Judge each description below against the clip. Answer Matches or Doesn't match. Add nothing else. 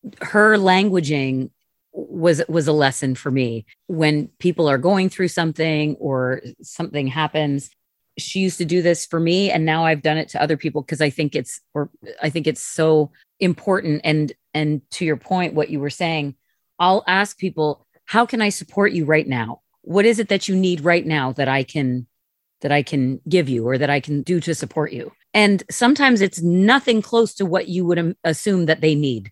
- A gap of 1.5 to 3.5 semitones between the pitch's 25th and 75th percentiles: Doesn't match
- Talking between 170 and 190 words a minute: Doesn't match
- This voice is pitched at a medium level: Matches